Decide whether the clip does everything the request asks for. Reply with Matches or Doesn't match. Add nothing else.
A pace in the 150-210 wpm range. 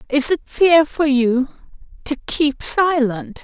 Doesn't match